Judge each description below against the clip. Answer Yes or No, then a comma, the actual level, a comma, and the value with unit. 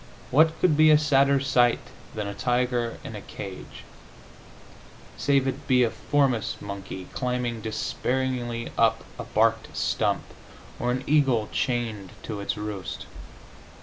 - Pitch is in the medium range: No, low, 120 Hz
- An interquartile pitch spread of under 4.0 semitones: Yes, average, 3.4 semitones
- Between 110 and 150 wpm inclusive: Yes, slow, 135 wpm